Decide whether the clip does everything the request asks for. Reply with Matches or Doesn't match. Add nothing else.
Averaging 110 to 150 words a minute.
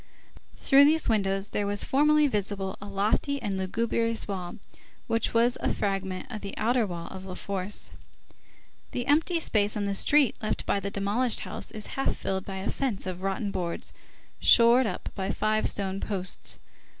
Doesn't match